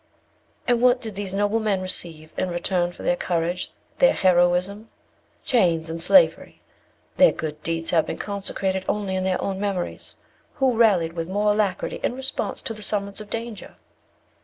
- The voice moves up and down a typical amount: Yes, average, 3.4 semitones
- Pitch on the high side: Yes, high, 195 Hz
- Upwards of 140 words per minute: Yes, average, 165 wpm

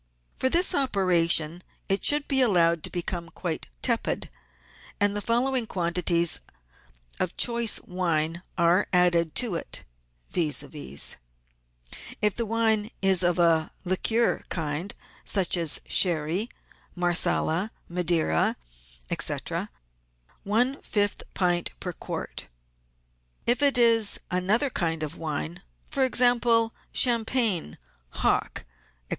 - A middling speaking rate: No, slow, 115 wpm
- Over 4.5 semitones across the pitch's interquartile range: Yes, average, 5.3 semitones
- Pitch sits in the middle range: Yes, medium, 180 Hz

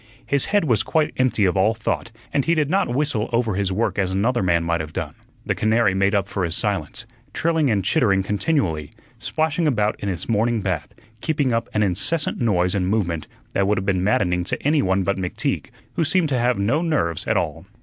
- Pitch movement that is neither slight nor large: No, wide, 5.7 semitones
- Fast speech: Yes, fast, 215 wpm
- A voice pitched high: No, low, 105 Hz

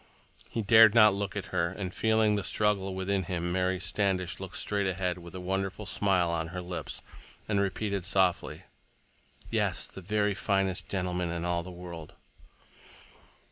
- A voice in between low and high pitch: No, very low, 95 Hz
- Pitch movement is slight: Yes, narrow, 2.1 semitones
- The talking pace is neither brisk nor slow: Yes, average, 160 wpm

